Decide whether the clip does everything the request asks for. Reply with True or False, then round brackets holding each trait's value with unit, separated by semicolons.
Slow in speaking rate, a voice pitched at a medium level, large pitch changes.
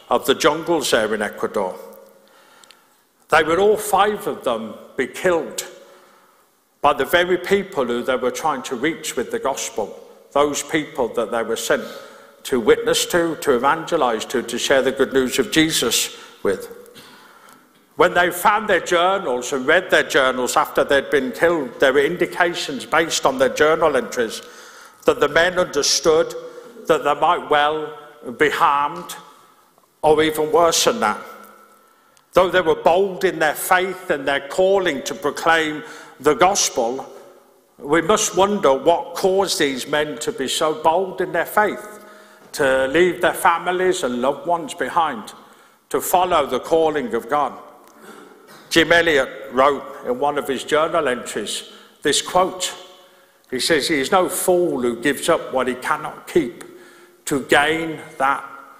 False (155 wpm; 175 Hz; 8.9 semitones)